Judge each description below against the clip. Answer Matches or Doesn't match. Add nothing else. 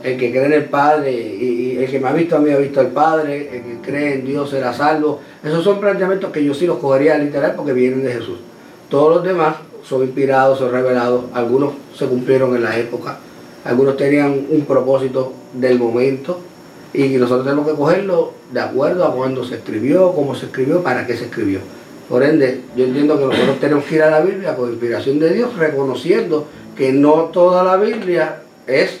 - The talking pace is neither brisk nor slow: Doesn't match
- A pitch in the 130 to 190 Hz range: Matches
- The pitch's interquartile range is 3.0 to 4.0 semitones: Matches